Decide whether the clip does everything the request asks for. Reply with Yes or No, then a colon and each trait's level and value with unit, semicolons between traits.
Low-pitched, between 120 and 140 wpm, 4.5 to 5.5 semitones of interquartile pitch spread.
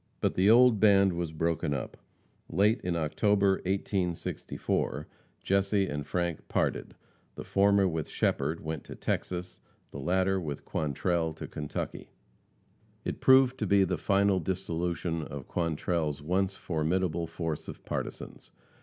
No: very low, 90 Hz; slow, 135 wpm; average, 3.4 semitones